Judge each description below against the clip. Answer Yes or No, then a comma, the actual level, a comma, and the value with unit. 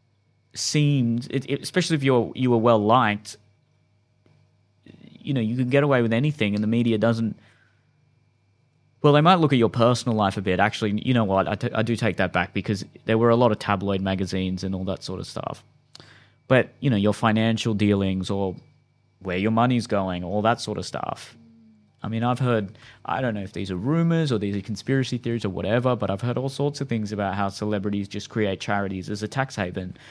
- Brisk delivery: Yes, fast, 215 wpm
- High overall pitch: No, low, 110 Hz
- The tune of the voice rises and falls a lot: No, average, 3.4 semitones